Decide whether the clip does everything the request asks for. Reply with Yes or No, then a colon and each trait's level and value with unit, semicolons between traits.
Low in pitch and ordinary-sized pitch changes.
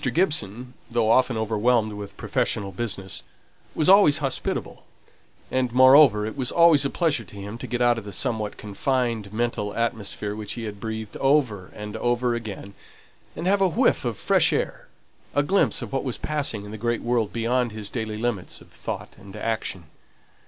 Yes: low, 115 Hz; average, 3.7 semitones